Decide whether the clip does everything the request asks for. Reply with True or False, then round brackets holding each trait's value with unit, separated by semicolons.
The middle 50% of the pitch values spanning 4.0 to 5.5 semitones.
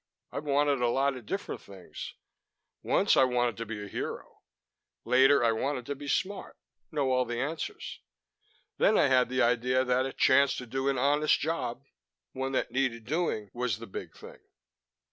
False (2.7 semitones)